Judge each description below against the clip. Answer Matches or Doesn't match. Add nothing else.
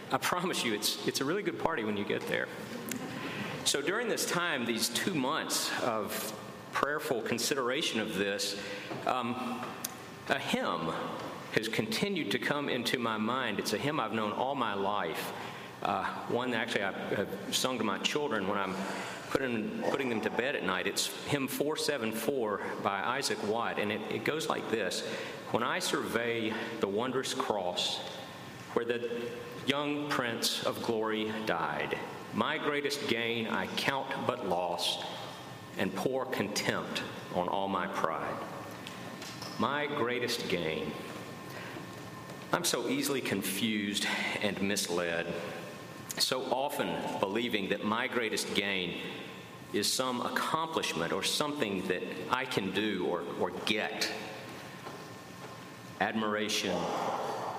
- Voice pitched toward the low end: Matches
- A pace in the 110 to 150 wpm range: Matches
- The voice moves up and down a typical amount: Matches